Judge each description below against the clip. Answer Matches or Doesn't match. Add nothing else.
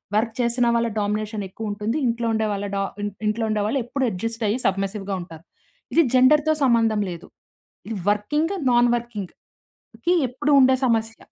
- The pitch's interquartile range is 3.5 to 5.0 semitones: Doesn't match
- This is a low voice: Doesn't match